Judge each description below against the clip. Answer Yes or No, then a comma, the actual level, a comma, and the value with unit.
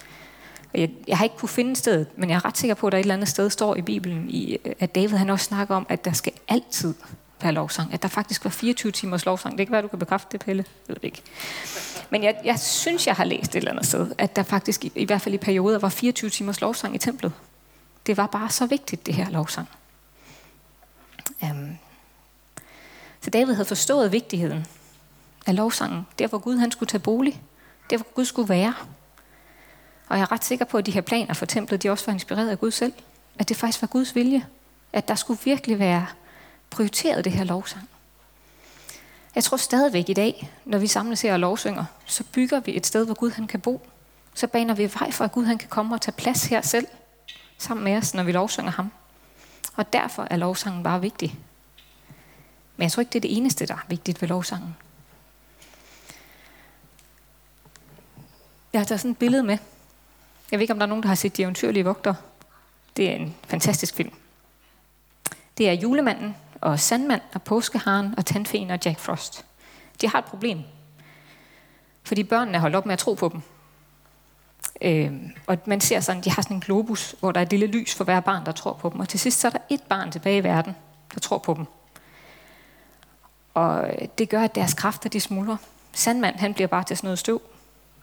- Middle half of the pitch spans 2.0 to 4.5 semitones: Yes, average, 4.2 semitones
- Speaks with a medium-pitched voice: No, high, 200 Hz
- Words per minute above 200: Yes, average, 210 wpm